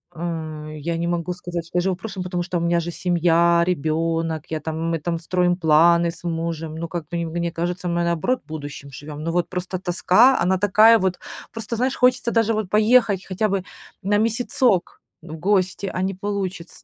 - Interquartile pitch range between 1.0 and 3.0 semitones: Yes, narrow, 2.6 semitones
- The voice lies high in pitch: No, medium, 175 Hz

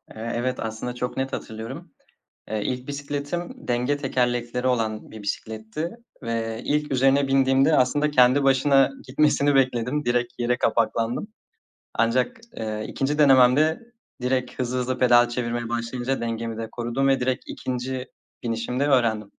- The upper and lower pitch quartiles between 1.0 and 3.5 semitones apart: Yes, narrow, 2.5 semitones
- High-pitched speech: No, low, 125 Hz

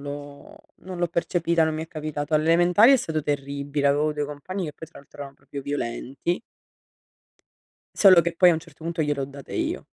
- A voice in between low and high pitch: Yes, medium, 155 Hz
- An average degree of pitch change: Yes, average, 3.0 semitones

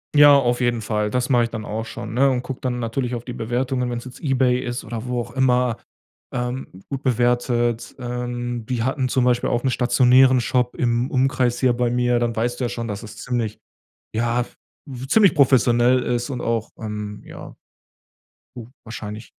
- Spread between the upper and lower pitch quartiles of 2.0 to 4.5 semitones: No, narrow, 1.3 semitones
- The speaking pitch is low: Yes, low, 120 Hz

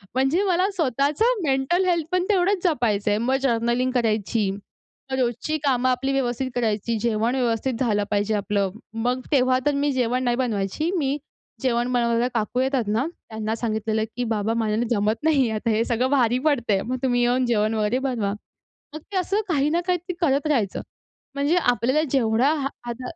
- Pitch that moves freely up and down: No, average, 3.8 semitones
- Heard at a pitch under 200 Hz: No, very high, 250 Hz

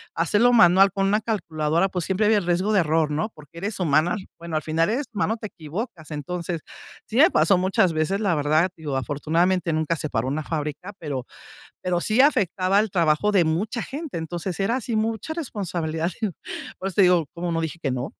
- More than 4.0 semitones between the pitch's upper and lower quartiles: Yes, average, 4.7 semitones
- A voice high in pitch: No, medium, 175 Hz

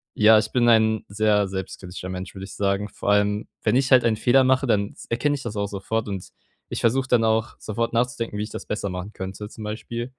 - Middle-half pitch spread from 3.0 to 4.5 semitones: No, narrow, 2.6 semitones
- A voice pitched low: Yes, low, 110 Hz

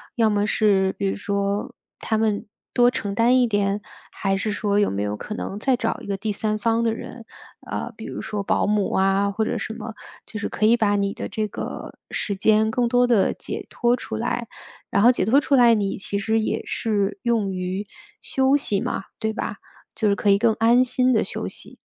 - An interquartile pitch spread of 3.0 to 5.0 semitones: No, narrow, 2.5 semitones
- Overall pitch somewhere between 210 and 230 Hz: Yes, high, 215 Hz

